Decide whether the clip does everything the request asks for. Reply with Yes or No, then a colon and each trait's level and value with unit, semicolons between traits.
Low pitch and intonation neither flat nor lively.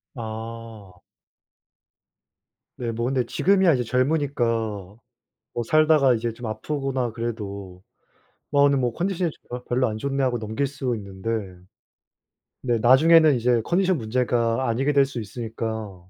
Yes: low, 120 Hz; average, 3.7 semitones